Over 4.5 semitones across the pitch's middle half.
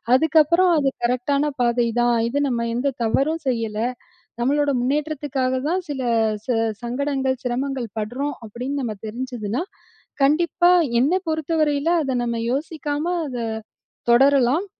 No: average, 3.5 semitones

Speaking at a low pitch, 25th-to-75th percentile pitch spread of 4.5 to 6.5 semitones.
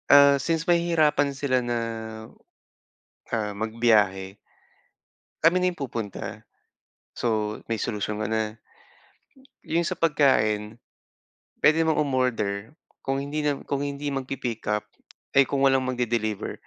Yes: low, 130 Hz; average, 4.8 semitones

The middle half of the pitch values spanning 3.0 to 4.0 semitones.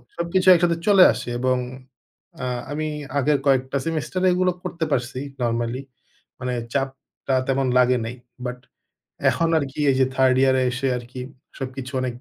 Yes: average, 3.5 semitones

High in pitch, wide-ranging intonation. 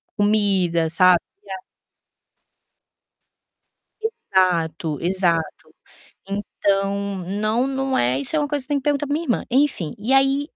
Yes: high, 205 Hz; wide, 6.9 semitones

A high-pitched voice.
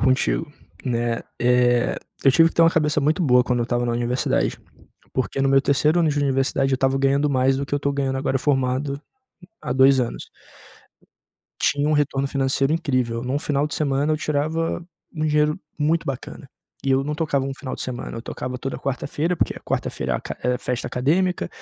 No: low, 135 Hz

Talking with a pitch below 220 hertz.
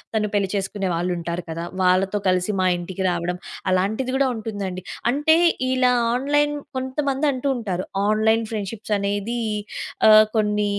Yes: high, 210 Hz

